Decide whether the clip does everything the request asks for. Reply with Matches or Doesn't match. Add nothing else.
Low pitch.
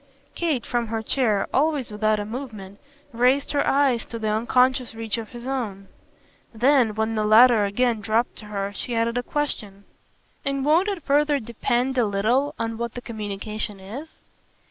Doesn't match